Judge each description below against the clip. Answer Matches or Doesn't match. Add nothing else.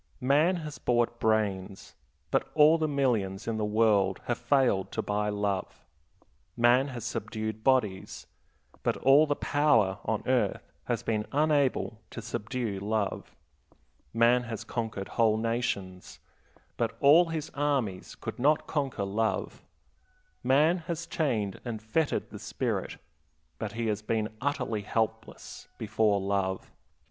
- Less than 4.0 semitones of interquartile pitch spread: Doesn't match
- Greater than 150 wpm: Doesn't match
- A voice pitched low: Matches